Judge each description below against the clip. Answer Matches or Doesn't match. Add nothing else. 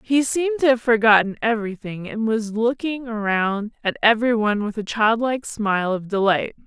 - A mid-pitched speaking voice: Doesn't match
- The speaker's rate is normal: Matches